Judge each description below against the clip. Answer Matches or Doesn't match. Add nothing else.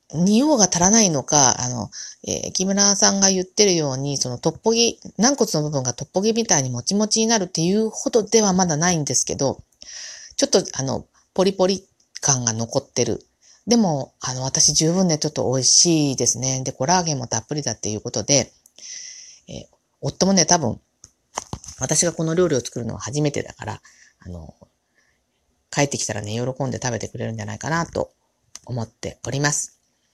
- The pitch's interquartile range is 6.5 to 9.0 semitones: Matches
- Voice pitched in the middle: Matches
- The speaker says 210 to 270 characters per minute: Doesn't match